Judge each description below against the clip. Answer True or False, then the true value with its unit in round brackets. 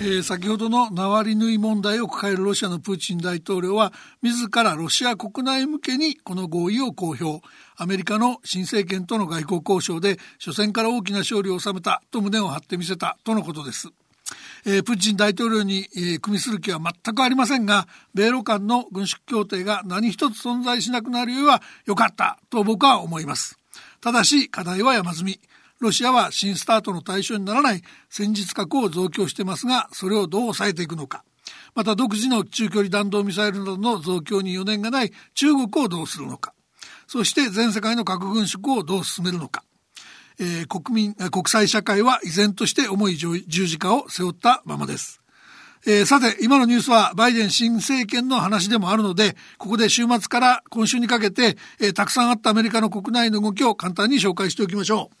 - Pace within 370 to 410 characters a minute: True (380 characters per minute)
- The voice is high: True (210 Hz)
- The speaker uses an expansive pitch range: False (3.5 semitones)